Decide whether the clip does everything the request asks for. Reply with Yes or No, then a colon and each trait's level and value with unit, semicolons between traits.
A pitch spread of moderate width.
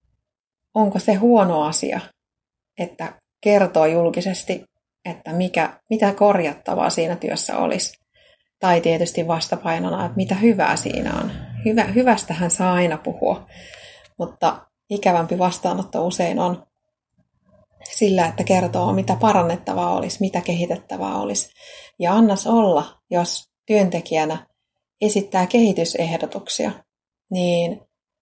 Yes: average, 3.3 semitones